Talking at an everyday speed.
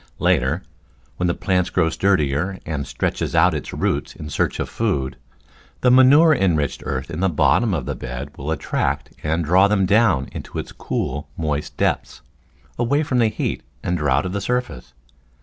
Yes: average, 175 wpm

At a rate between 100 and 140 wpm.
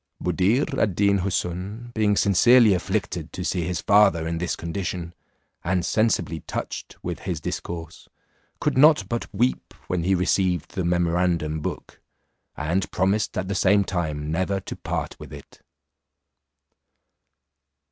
Yes: slow, 135 wpm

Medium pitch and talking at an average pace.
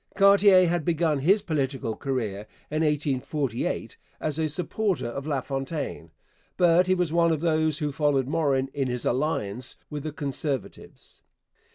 Yes: medium, 150 Hz; average, 145 wpm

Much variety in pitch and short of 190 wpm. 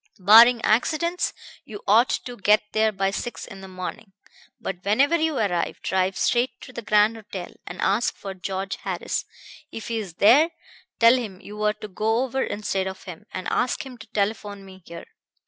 No: average, 3.4 semitones; average, 180 wpm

